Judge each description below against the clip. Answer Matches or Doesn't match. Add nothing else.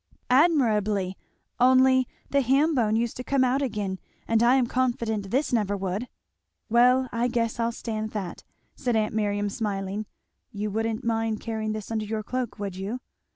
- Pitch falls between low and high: Doesn't match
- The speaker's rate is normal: Matches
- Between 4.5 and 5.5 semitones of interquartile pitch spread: Doesn't match